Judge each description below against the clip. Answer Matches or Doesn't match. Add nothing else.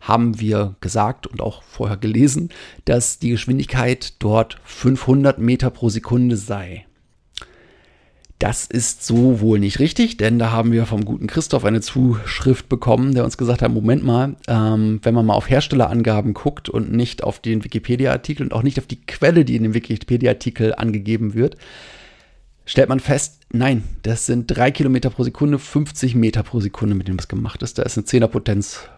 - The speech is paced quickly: Doesn't match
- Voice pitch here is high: Doesn't match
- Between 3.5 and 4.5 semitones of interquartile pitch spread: Doesn't match